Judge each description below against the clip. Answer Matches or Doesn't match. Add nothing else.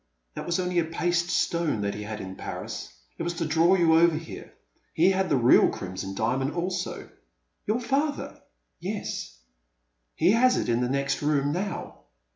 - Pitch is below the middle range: Doesn't match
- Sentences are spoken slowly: Doesn't match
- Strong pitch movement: Matches